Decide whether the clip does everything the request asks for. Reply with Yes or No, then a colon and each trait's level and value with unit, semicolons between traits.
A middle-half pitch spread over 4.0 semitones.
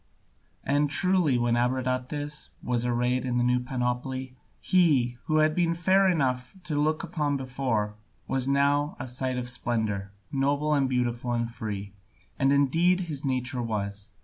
No: average, 3.2 semitones